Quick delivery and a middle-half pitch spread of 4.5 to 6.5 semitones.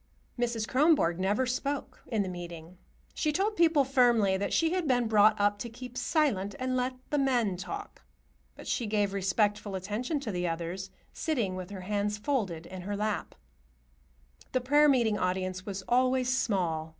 No: average, 165 wpm; average, 5.2 semitones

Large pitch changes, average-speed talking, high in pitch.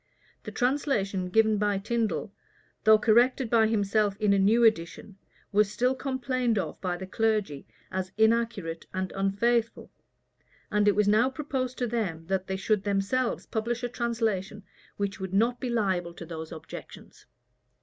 No: average, 3.5 semitones; average, 155 wpm; high, 215 Hz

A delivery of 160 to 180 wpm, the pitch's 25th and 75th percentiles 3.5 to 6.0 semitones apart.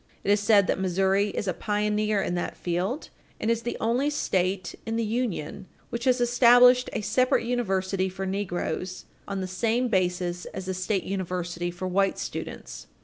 Yes: average, 175 wpm; average, 3.8 semitones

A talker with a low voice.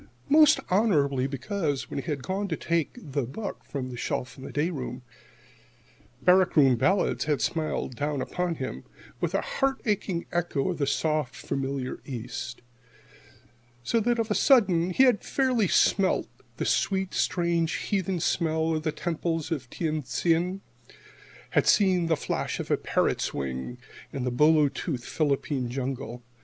No: medium, 160 Hz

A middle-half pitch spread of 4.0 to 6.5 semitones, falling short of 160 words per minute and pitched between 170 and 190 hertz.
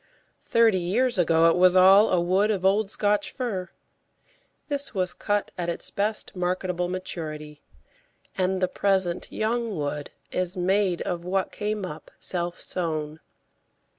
No: average, 2.9 semitones; average, 140 wpm; medium, 185 Hz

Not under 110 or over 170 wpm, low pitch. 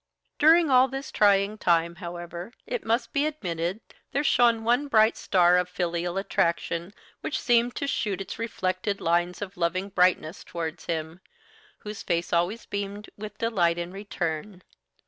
No: average, 150 wpm; high, 195 Hz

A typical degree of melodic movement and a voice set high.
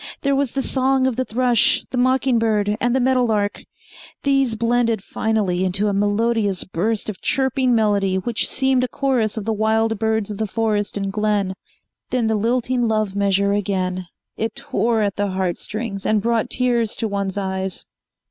Yes: average, 3.2 semitones; high, 220 Hz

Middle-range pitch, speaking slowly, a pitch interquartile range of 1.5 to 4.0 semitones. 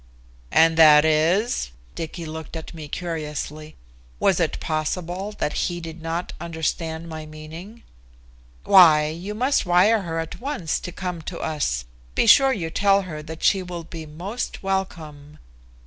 No: medium, 165 Hz; average, 150 wpm; average, 3.1 semitones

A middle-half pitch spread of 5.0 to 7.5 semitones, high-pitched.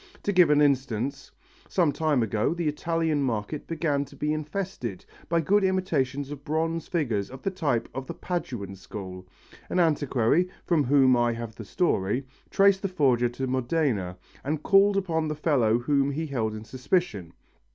No: wide, 5.6 semitones; medium, 145 Hz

